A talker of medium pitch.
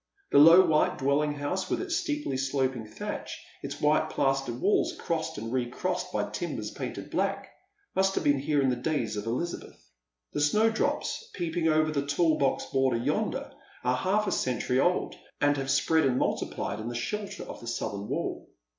Yes: medium, 145 Hz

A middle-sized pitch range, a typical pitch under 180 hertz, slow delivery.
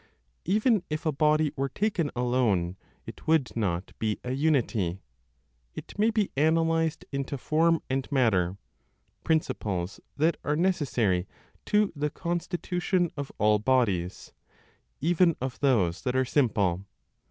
No: wide, 7.1 semitones; medium, 140 Hz; slow, 130 wpm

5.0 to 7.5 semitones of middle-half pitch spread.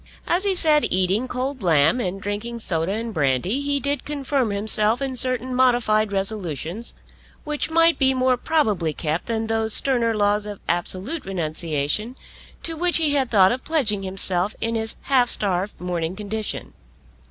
Yes: wide, 5.5 semitones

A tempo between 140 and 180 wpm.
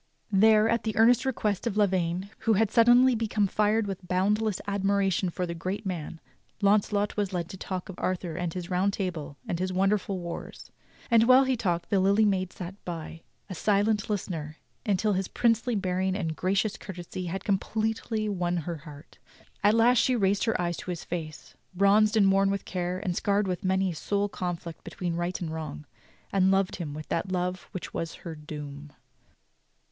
No: average, 190 wpm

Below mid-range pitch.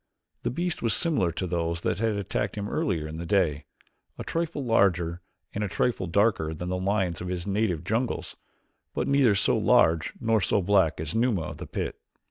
Yes: very low, 95 Hz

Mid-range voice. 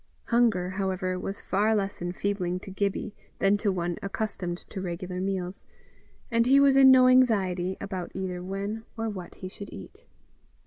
No: high, 195 Hz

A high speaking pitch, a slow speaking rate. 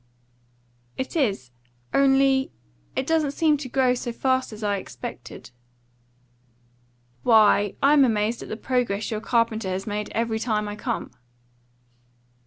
Yes: high, 230 Hz; slow, 130 wpm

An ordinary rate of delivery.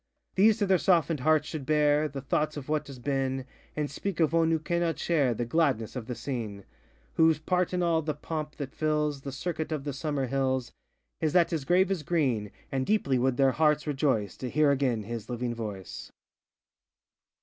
Yes: average, 195 wpm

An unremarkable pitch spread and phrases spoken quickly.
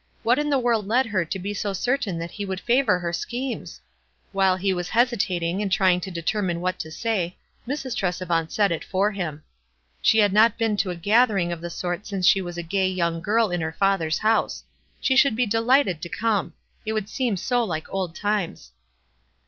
Yes: average, 4.3 semitones; fast, 210 wpm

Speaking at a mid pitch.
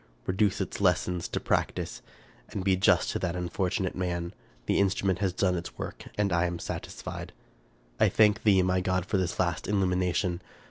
No: very low, 90 Hz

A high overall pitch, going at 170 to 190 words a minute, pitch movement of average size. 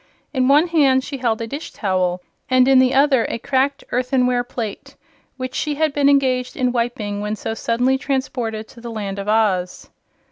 Yes: very high, 250 Hz; average, 185 wpm; average, 3.3 semitones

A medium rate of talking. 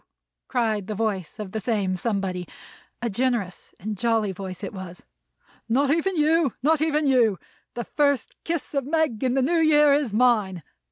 Yes: average, 170 wpm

